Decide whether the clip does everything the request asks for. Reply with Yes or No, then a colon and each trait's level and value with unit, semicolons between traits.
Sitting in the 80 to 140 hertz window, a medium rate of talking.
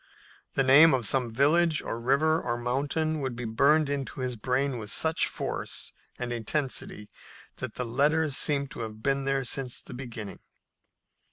Yes: low, 135 Hz; average, 165 wpm